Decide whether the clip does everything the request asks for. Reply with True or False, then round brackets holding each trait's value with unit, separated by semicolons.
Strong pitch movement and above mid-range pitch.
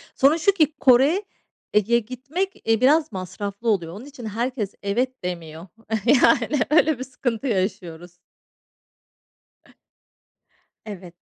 True (5.9 semitones; 240 Hz)